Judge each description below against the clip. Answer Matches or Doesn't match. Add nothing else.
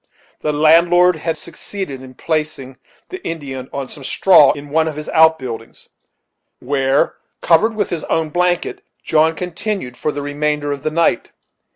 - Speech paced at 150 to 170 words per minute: Matches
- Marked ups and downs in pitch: Doesn't match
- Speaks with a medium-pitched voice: Matches